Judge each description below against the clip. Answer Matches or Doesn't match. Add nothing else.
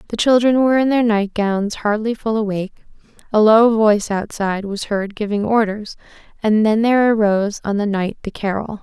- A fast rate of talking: Doesn't match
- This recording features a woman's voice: Matches